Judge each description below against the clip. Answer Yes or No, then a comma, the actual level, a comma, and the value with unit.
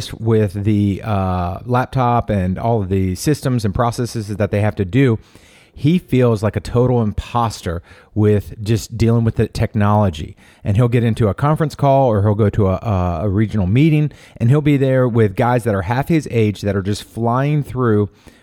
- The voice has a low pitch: Yes, low, 110 Hz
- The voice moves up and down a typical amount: Yes, average, 3.3 semitones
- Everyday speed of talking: Yes, average, 190 wpm